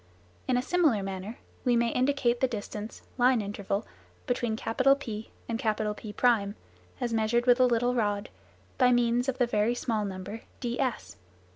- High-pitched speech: Yes, high, 235 Hz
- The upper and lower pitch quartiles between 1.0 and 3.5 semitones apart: Yes, average, 2.8 semitones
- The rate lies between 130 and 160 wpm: Yes, average, 150 wpm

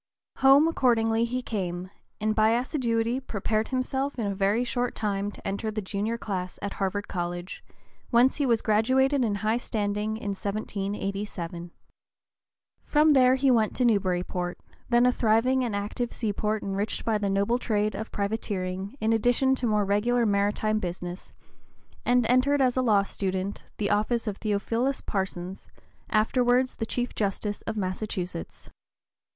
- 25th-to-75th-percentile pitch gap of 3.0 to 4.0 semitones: Yes, average, 3.4 semitones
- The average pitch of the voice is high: Yes, high, 215 Hz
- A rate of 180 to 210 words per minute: No, average, 150 wpm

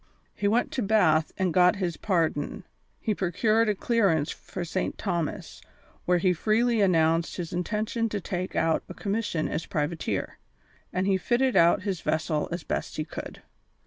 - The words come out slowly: No, average, 165 wpm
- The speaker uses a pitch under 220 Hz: Yes, medium, 185 Hz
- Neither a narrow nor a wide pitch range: Yes, average, 4.2 semitones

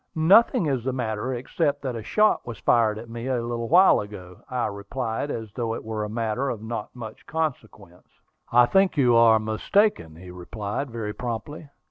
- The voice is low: Yes, low, 115 Hz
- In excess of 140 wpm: Yes, average, 185 wpm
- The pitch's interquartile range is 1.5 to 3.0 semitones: No, average, 3.8 semitones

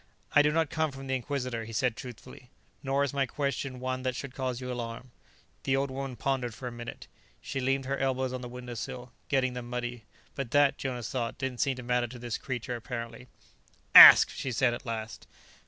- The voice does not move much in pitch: Yes, narrow, 1.9 semitones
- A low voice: Yes, low, 125 Hz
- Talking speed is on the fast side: Yes, fast, 210 wpm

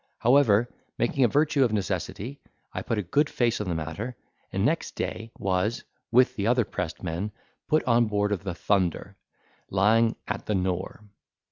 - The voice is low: Yes, low, 105 Hz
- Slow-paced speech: No, average, 170 wpm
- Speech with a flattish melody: No, average, 4.3 semitones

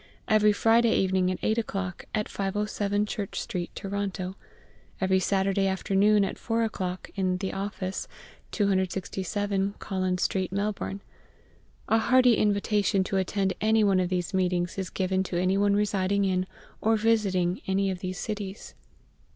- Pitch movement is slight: Yes, narrow, 1.8 semitones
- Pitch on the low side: No, high, 195 Hz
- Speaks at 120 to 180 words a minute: Yes, average, 145 wpm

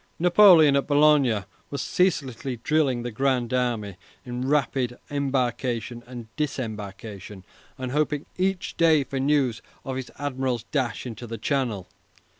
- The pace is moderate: No, slow, 130 wpm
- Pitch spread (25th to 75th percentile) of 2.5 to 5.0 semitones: Yes, average, 3.5 semitones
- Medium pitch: No, low, 130 Hz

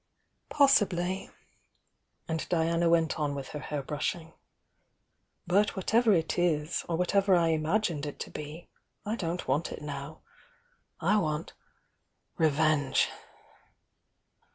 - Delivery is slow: Yes, slow, 125 wpm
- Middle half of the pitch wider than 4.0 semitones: No, average, 3.1 semitones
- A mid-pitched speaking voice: Yes, medium, 165 Hz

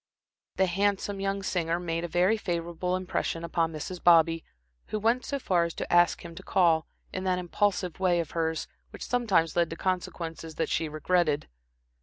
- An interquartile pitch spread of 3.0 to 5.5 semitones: No, narrow, 2.4 semitones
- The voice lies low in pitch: No, medium, 175 Hz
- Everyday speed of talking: Yes, average, 180 wpm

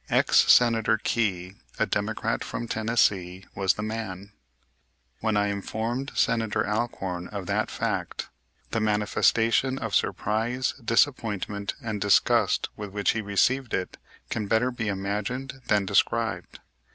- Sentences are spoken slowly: Yes, slow, 130 wpm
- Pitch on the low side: Yes, low, 110 Hz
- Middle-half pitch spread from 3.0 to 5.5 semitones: No, narrow, 2.5 semitones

